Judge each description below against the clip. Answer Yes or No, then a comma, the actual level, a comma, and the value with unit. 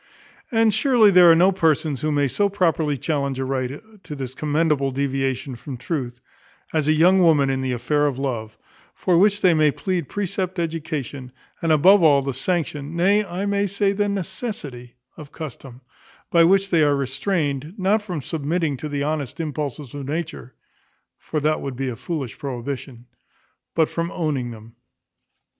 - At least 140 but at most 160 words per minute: No, average, 170 wpm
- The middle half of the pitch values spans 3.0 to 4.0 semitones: No, average, 4.8 semitones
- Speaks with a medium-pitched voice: Yes, medium, 155 Hz